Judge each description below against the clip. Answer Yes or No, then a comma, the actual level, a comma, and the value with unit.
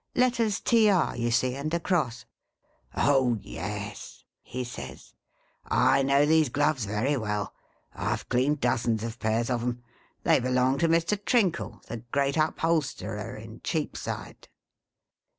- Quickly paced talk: No, average, 145 wpm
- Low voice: Yes, low, 130 Hz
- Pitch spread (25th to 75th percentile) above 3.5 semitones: Yes, average, 5.2 semitones